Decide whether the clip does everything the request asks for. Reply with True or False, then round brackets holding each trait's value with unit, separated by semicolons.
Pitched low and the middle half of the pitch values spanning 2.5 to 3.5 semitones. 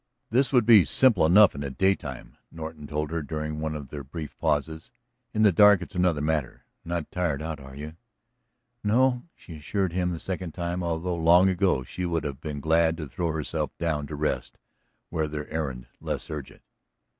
True (80 Hz; 3.2 semitones)